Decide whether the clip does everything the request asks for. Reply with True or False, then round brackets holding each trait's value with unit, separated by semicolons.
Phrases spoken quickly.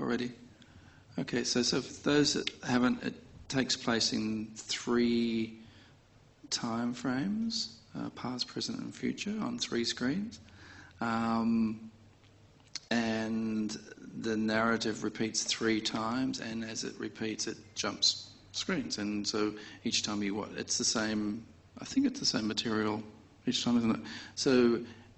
False (135 wpm)